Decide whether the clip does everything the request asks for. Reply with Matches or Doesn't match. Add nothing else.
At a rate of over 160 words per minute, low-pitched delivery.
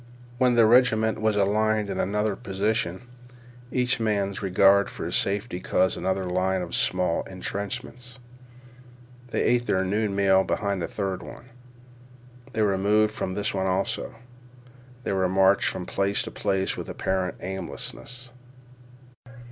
Doesn't match